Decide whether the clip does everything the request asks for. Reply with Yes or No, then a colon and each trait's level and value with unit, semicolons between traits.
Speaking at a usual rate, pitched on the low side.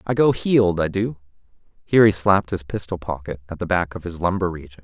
No: fast, 225 wpm; very low, 90 Hz